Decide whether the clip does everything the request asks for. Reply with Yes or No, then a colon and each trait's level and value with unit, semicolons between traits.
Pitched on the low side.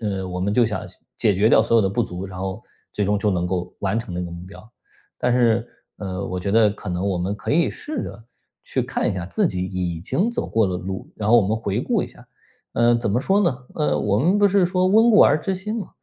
Yes: low, 105 Hz